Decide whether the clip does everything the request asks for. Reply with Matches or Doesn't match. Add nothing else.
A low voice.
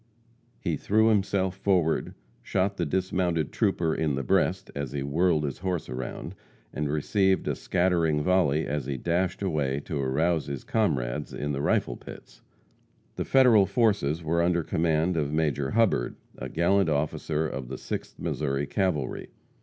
Matches